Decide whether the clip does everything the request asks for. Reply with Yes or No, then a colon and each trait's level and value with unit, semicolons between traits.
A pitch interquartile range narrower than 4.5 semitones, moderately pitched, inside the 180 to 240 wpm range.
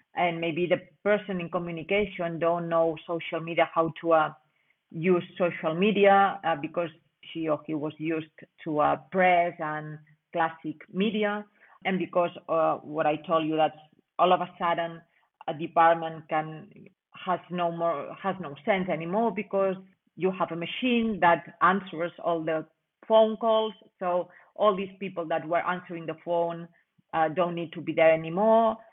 No: average, 2.7 semitones; medium, 170 Hz; average, 160 wpm